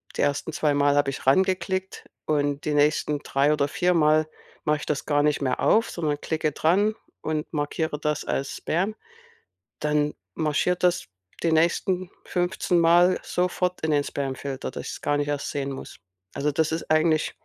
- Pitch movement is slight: No, average, 3.0 semitones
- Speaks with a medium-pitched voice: Yes, medium, 150 Hz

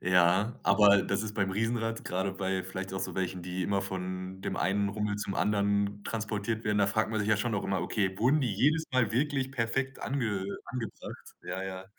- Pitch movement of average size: Yes, average, 3.0 semitones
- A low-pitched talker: Yes, low, 100 Hz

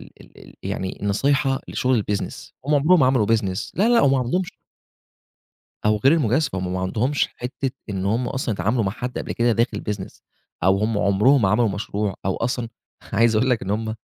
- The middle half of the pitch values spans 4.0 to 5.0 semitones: Yes, average, 4.4 semitones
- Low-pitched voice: Yes, low, 115 Hz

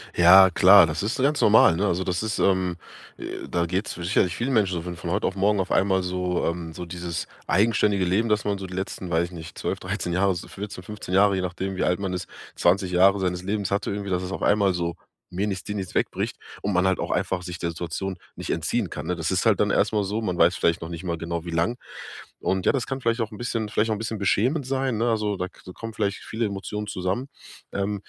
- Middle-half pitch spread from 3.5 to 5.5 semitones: No, average, 2.7 semitones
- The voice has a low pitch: Yes, very low, 95 Hz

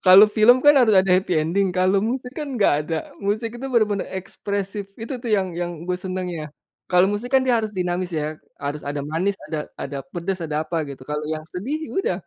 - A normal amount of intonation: Yes, average, 4.6 semitones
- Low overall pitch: No, high, 190 Hz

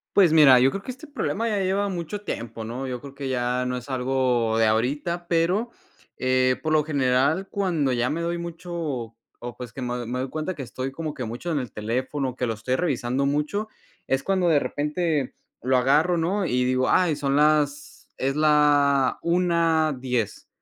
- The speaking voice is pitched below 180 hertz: Yes, medium, 140 Hz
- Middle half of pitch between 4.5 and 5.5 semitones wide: Yes, average, 4.9 semitones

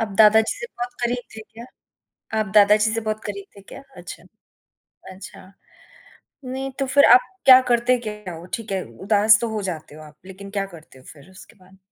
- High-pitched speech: Yes, high, 210 Hz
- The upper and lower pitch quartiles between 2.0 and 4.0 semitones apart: Yes, average, 3.7 semitones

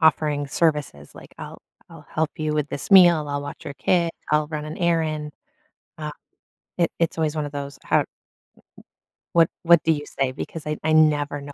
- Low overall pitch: No, medium, 150 Hz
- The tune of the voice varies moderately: No, narrow, 1.8 semitones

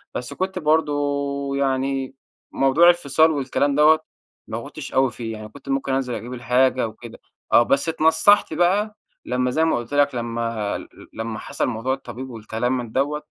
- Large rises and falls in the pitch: No, average, 4.0 semitones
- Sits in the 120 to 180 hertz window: Yes, low, 135 Hz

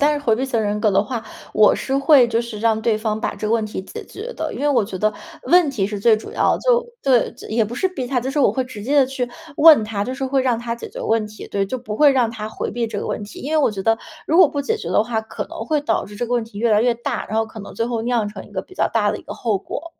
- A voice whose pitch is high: Yes, high, 235 Hz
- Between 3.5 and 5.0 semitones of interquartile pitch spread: Yes, average, 3.9 semitones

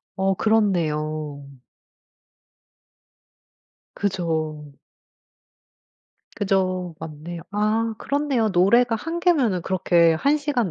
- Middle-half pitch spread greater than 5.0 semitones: Yes, wide, 5.6 semitones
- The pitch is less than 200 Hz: Yes, high, 190 Hz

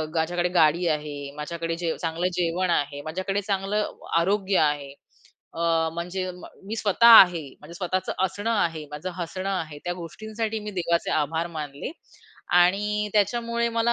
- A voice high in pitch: No, medium, 175 Hz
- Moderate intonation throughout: Yes, average, 3.7 semitones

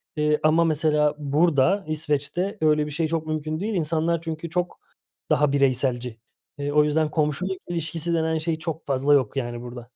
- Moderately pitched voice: Yes, medium, 155 Hz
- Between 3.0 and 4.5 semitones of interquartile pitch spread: No, narrow, 2.4 semitones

